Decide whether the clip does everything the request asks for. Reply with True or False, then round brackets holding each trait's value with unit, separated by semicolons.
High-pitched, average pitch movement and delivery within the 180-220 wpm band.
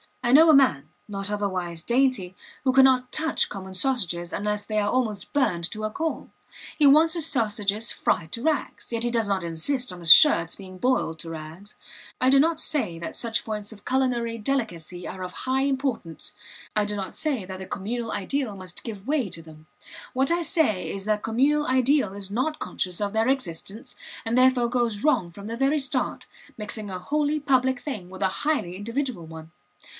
False (225 Hz; 6.0 semitones; 195 wpm)